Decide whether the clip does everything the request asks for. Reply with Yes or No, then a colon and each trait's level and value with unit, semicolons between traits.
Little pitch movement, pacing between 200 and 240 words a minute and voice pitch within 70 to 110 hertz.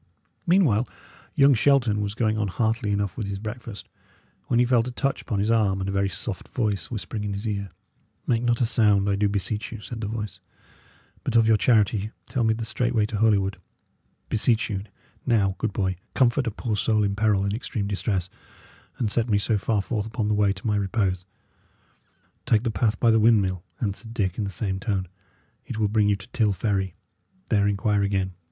Yes: narrow, 2.3 semitones; fast, 205 wpm; low, 105 Hz